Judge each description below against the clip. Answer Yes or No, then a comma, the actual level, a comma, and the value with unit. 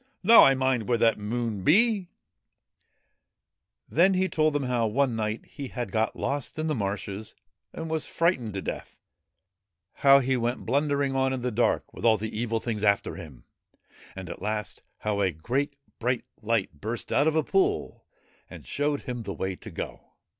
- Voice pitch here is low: Yes, low, 120 Hz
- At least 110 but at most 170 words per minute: No, average, 185 wpm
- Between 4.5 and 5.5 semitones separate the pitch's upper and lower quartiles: Yes, average, 5.0 semitones